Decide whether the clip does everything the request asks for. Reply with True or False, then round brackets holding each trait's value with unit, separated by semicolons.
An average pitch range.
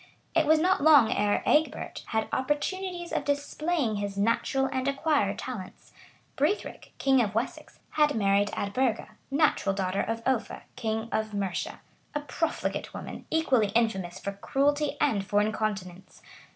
False (6.3 semitones)